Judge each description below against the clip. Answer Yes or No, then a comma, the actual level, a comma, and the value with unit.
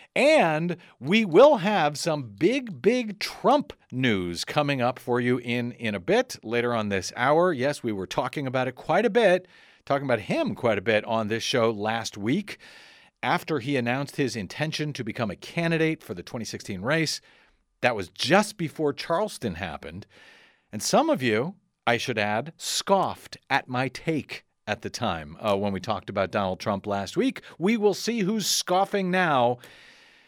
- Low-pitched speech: No, medium, 145 Hz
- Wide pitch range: Yes, wide, 7.8 semitones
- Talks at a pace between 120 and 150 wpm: No, average, 175 wpm